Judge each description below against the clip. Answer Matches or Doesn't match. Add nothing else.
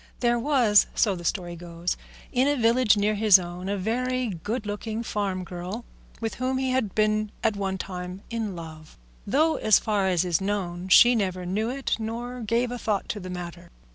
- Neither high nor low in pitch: Doesn't match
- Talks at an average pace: Matches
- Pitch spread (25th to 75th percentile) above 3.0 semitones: Matches